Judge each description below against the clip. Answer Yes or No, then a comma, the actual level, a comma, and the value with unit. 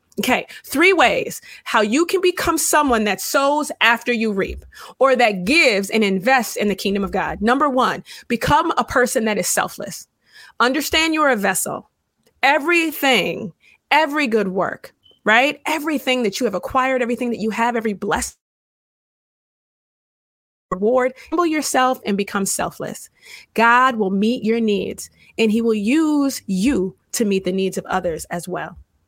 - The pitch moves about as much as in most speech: No, wide, 5.7 semitones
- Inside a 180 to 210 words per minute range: No, average, 155 wpm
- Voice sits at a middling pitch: No, high, 240 Hz